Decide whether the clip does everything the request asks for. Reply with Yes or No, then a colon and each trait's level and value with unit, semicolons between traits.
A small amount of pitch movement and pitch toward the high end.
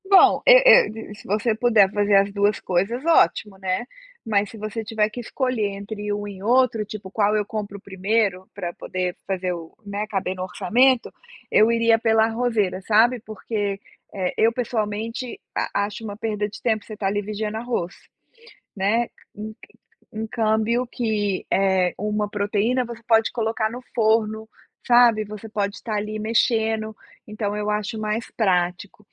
Yes: narrow, 1.9 semitones; high, 215 Hz